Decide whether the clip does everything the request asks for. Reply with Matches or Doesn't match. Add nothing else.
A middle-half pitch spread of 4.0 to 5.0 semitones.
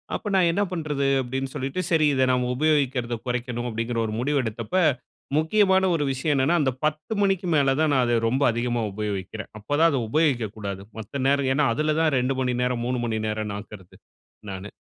Matches